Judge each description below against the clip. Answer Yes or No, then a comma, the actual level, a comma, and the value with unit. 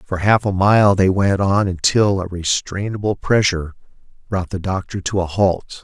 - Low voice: Yes, very low, 95 Hz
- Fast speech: No, average, 175 wpm